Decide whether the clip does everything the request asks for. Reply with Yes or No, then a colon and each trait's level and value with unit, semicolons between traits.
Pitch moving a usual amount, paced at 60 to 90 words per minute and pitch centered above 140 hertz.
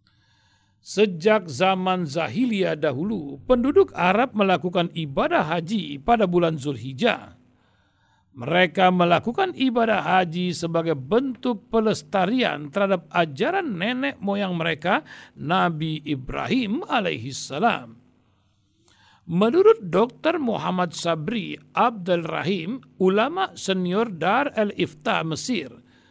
No: wide, 6.2 semitones; slow, 85 wpm; medium, 185 Hz